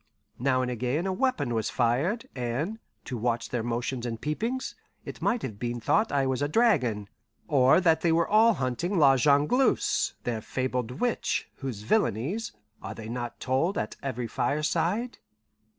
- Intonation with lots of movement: Yes, wide, 6.2 semitones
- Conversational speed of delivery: Yes, average, 165 wpm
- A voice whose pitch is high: No, low, 130 Hz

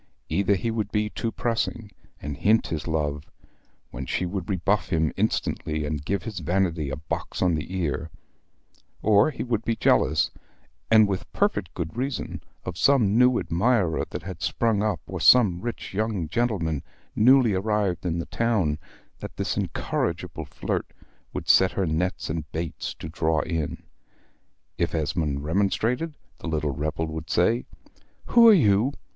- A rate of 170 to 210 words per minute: No, average, 160 wpm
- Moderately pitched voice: No, very low, 95 Hz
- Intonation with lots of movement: Yes, wide, 5.7 semitones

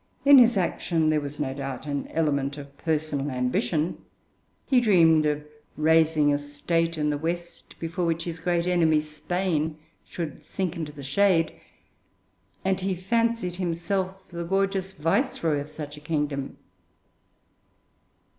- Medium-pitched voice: Yes, medium, 160 Hz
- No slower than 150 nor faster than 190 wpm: No, average, 140 wpm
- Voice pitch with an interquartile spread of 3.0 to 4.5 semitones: Yes, average, 3.4 semitones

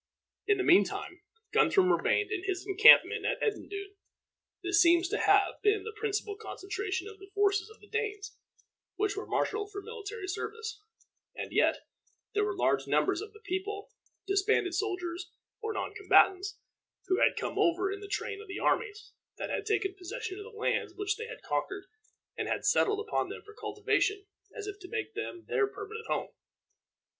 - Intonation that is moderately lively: No, narrow, 1.7 semitones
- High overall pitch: Yes, very high, 410 Hz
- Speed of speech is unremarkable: Yes, average, 180 wpm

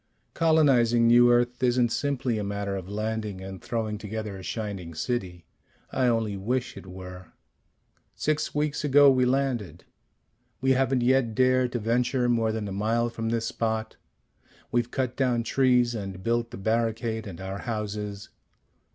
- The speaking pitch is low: Yes, low, 115 Hz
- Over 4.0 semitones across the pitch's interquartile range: No, average, 3.3 semitones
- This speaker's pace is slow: No, average, 155 wpm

